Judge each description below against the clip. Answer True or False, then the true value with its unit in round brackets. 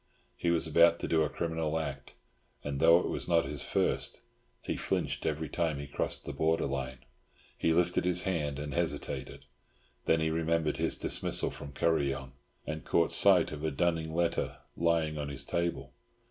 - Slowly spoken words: False (175 wpm)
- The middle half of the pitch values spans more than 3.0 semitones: False (2.5 semitones)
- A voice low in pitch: True (80 Hz)